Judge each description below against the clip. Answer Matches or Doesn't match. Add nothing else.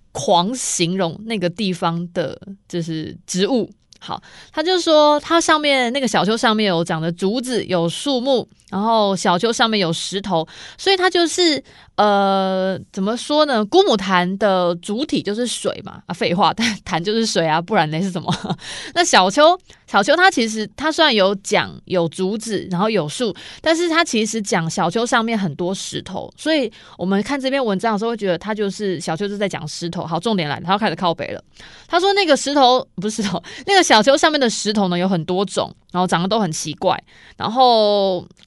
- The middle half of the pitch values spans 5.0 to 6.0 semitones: Matches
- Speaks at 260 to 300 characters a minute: Matches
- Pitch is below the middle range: Doesn't match